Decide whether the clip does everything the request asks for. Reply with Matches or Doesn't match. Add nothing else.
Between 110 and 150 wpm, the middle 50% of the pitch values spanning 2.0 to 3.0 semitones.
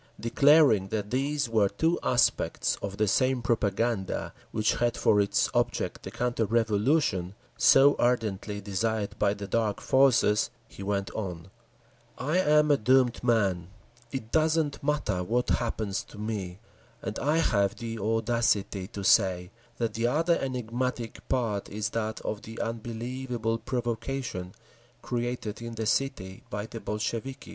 Doesn't match